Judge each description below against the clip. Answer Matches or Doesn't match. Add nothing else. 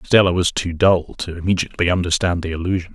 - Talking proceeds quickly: Doesn't match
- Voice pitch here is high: Doesn't match